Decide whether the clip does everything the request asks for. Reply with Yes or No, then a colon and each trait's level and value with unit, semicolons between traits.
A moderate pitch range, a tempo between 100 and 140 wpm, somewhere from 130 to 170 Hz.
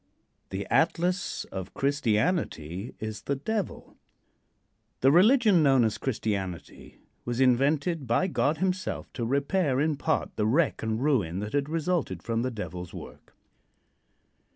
No: wide, 7.0 semitones; slow, 135 wpm; low, 135 Hz